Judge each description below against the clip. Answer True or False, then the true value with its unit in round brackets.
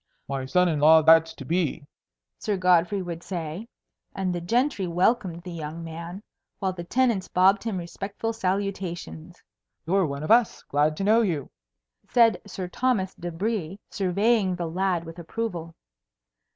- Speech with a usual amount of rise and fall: True (3.3 semitones)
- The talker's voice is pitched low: False (180 Hz)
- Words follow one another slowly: False (155 wpm)